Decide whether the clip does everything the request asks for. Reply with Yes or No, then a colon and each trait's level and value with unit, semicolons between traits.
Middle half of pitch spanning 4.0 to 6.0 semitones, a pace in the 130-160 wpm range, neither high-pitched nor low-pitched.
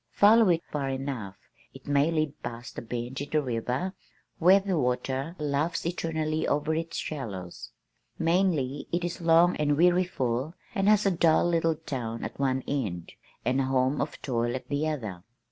No: average, 4.6 semitones; average, 170 wpm; medium, 145 Hz